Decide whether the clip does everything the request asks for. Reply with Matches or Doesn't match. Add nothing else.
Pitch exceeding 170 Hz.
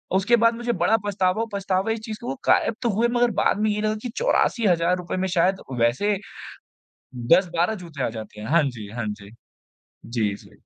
Matches